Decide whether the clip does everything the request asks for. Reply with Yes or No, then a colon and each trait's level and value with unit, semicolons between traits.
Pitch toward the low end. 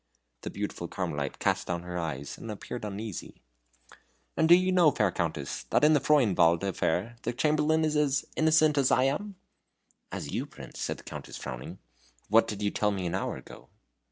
Yes: low, 110 Hz